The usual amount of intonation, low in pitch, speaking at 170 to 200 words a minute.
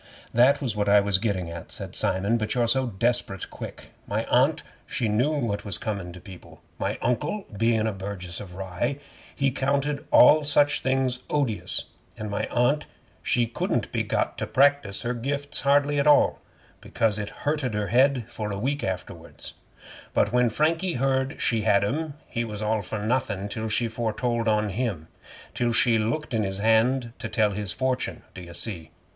Yes: average, 4.5 semitones; low, 115 Hz; average, 185 wpm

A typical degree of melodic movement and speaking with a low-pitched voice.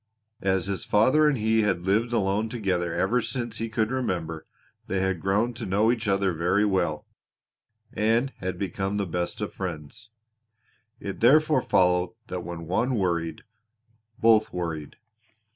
Yes: average, 4.0 semitones; low, 100 Hz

